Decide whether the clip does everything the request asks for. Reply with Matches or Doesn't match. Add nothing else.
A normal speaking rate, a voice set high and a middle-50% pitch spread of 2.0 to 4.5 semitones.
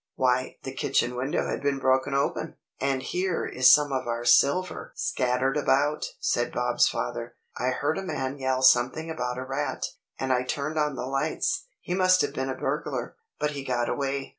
Doesn't match